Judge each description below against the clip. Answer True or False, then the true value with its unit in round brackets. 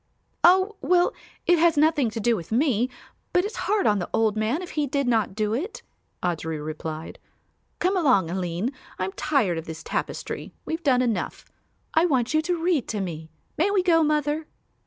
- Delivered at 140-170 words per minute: False (185 wpm)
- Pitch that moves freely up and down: True (8.7 semitones)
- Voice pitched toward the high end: True (265 Hz)